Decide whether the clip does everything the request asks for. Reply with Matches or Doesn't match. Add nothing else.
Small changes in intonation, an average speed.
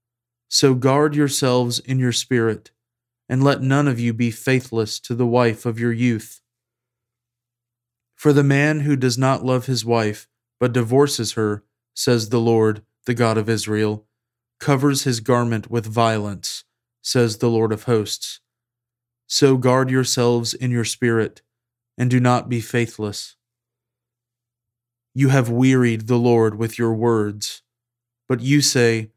Matches